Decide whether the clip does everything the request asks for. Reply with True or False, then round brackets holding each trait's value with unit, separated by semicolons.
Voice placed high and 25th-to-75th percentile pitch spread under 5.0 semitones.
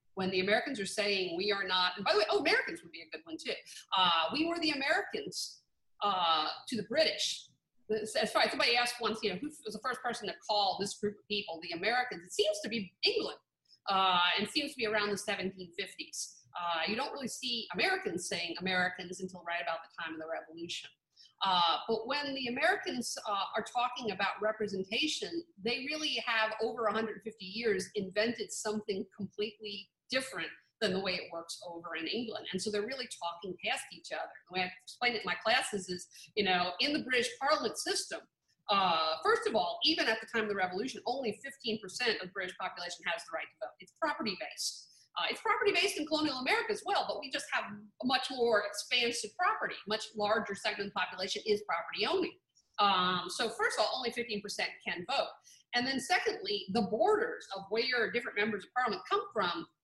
False (215 Hz; 5.5 semitones)